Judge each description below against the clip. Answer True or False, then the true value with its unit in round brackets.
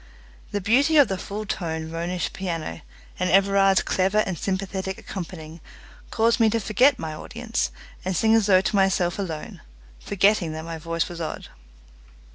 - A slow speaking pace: False (160 wpm)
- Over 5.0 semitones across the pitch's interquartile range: False (4.1 semitones)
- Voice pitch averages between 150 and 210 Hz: True (190 Hz)